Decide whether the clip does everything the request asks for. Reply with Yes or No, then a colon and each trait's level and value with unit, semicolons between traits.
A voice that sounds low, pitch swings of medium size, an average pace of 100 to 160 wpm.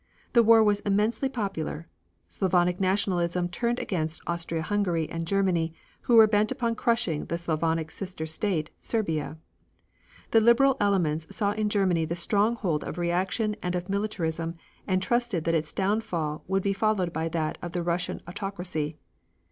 No: medium, 185 Hz; average, 4.0 semitones; average, 150 wpm